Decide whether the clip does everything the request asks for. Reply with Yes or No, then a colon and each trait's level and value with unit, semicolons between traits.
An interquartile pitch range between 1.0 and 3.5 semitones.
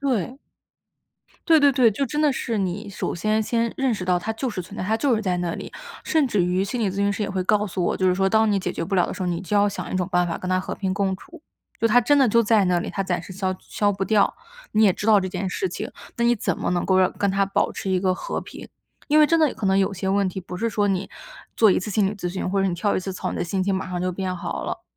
Yes: average, 3.0 semitones